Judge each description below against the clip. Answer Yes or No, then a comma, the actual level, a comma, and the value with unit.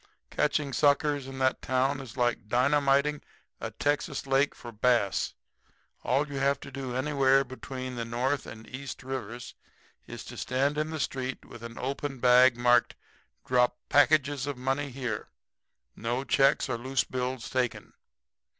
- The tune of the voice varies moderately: No, narrow, 2.2 semitones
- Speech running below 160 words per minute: Yes, average, 150 wpm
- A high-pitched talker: No, low, 130 Hz